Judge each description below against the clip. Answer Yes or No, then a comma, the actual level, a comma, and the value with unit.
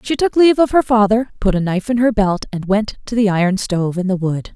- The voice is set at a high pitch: Yes, high, 210 Hz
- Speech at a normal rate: No, fast, 275 wpm